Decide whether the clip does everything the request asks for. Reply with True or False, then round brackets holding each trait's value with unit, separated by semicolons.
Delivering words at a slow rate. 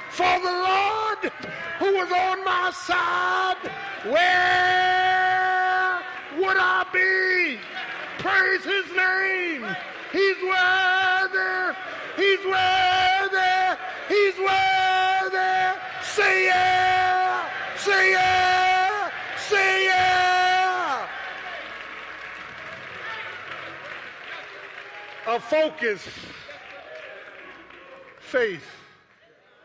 True (65 wpm)